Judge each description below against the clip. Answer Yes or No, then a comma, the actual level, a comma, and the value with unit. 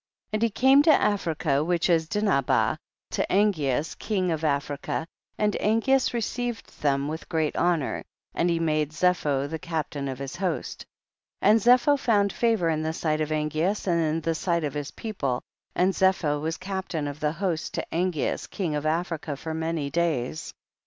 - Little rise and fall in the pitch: No, average, 4.3 semitones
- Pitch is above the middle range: No, medium, 165 Hz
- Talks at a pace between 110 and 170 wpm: No, average, 180 wpm